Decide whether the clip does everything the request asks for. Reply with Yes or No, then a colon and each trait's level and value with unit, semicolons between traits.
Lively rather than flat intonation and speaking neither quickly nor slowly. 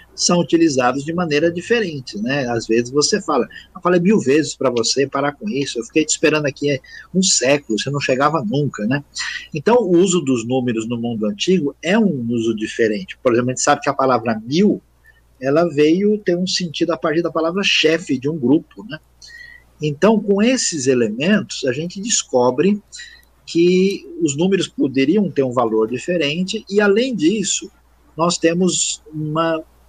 Yes: wide, 5.9 semitones; average, 175 wpm